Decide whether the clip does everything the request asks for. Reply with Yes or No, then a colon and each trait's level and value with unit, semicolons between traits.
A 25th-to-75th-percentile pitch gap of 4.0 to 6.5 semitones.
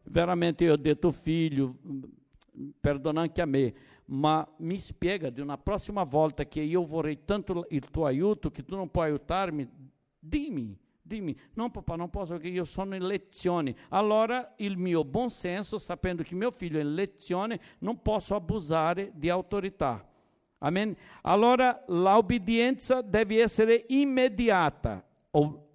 Yes: average, 5.2 semitones